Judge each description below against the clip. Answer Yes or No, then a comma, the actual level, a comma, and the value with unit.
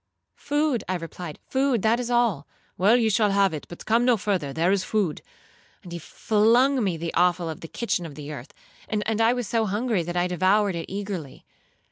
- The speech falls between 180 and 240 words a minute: Yes, average, 185 wpm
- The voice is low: No, high, 200 Hz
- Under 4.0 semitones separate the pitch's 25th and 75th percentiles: No, average, 4.9 semitones